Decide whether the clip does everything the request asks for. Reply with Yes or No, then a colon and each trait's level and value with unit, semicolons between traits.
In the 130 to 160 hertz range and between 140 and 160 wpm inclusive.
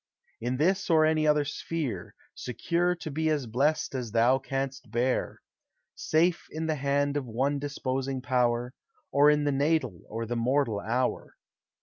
Yes: medium, 140 Hz; average, 155 wpm